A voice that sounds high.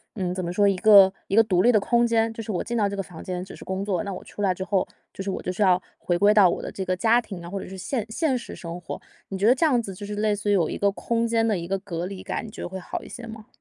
Yes: high, 200 Hz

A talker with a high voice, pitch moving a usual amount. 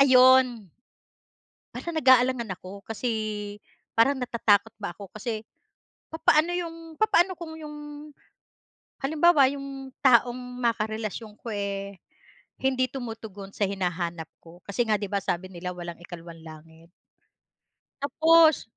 No: high, 230 Hz; wide, 5.9 semitones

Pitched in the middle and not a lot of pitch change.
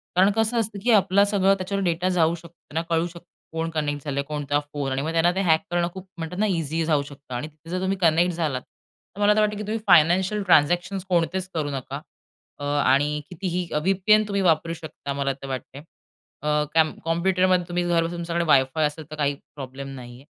No: medium, 165 Hz; average, 3.9 semitones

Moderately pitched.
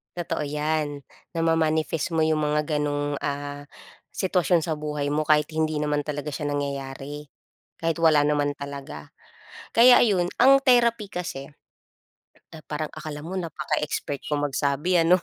Yes: medium, 150 Hz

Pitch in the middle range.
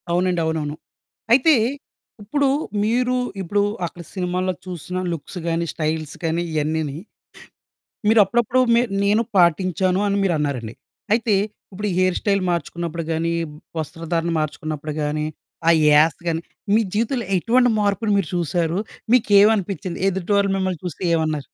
Yes: medium, 180 Hz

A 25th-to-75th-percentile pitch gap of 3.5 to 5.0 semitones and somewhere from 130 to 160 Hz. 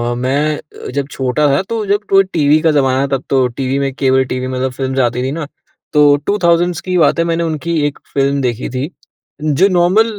Yes: average, 4.2 semitones; medium, 140 Hz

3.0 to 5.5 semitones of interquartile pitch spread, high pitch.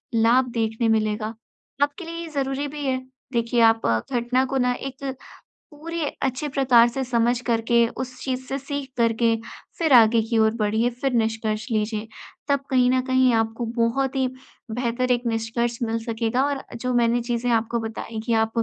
No: narrow, 2.5 semitones; high, 240 Hz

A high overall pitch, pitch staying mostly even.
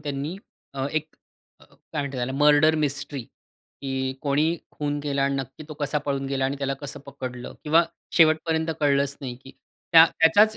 No: medium, 140 Hz; narrow, 2.2 semitones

